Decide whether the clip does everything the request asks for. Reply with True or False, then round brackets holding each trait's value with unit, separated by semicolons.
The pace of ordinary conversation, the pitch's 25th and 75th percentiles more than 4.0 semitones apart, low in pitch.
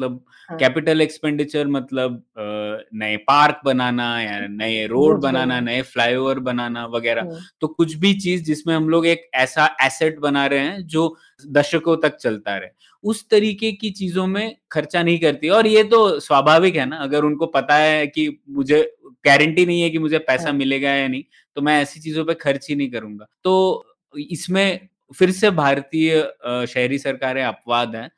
False (170 wpm; 4.5 semitones; 150 Hz)